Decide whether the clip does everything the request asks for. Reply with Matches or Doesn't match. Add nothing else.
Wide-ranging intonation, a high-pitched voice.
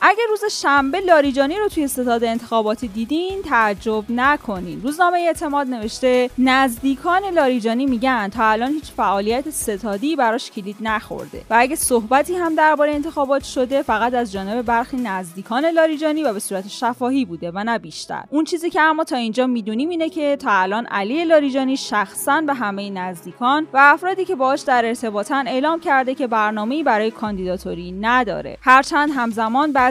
Doesn't match